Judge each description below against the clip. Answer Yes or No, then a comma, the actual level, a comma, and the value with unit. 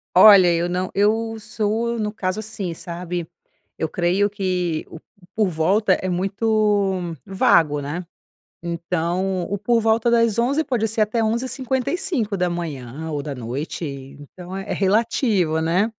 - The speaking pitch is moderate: No, high, 195 Hz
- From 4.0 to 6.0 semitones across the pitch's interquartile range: Yes, average, 4.3 semitones